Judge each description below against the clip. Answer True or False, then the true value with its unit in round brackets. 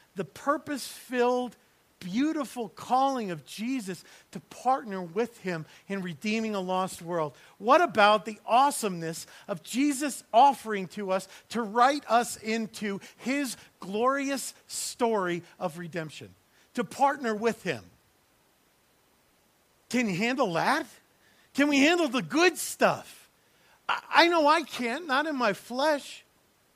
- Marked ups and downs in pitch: True (6.5 semitones)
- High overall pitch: True (230 Hz)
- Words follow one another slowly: True (125 wpm)